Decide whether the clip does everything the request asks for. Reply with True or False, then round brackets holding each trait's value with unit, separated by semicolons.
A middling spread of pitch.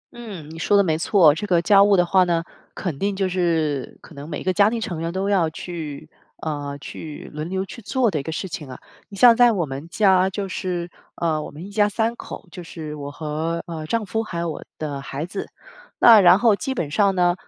True (4.2 semitones)